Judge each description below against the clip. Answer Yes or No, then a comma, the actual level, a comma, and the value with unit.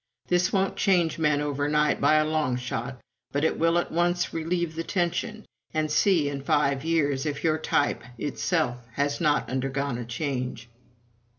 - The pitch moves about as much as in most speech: Yes, average, 3.1 semitones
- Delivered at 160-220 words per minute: Yes, average, 170 wpm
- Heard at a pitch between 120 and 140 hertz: No, medium, 150 Hz